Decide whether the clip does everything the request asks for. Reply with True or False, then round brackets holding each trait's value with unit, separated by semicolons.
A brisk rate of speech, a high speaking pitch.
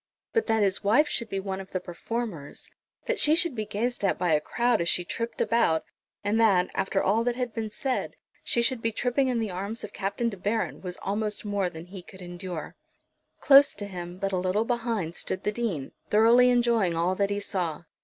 True (215 wpm; 205 Hz)